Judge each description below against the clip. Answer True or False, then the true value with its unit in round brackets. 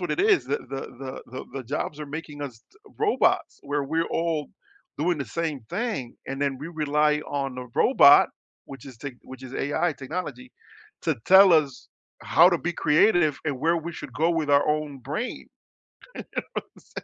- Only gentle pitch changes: False (3.6 semitones)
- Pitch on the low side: False (150 Hz)